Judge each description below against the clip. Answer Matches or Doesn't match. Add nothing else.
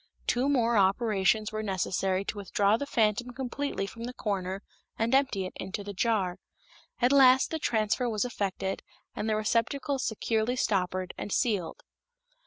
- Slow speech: Doesn't match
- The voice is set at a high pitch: Matches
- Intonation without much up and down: Doesn't match